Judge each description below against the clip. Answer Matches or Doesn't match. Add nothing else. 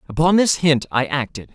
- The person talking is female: Doesn't match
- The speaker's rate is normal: Matches